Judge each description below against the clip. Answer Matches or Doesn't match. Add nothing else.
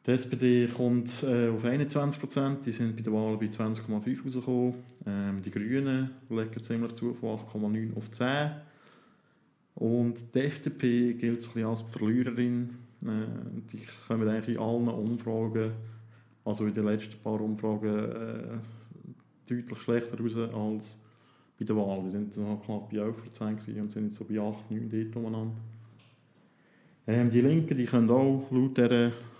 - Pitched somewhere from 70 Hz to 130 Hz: Matches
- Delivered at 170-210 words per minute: Doesn't match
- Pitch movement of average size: Doesn't match